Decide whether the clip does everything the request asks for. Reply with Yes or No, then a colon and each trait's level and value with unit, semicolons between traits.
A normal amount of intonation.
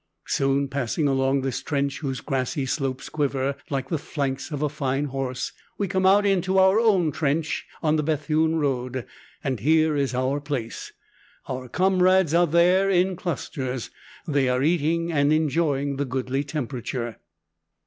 Yes: average, 3.6 semitones